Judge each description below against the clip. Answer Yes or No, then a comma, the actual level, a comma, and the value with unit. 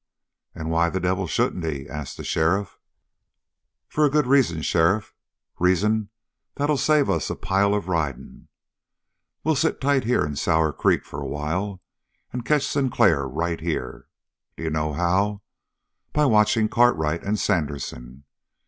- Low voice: Yes, very low, 95 Hz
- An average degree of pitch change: No, wide, 5.9 semitones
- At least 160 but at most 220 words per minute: No, average, 145 wpm